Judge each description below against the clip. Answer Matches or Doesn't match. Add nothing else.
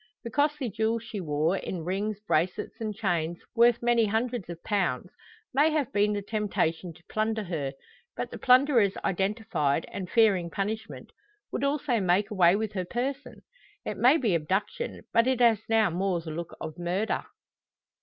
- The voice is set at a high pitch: Matches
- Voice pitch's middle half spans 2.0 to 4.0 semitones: Doesn't match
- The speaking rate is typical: Matches